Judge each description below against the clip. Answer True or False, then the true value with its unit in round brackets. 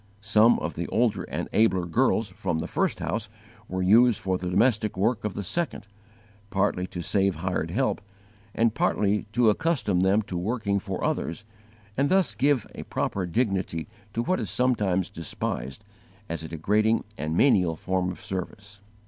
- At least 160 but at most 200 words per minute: True (165 wpm)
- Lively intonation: False (4.0 semitones)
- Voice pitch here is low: True (100 Hz)